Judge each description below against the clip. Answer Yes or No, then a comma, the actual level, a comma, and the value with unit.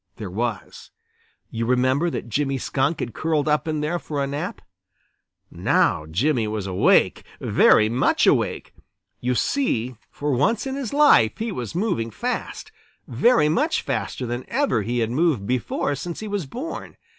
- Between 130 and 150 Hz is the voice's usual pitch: Yes, medium, 140 Hz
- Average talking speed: Yes, average, 160 wpm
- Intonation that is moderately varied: No, wide, 6.8 semitones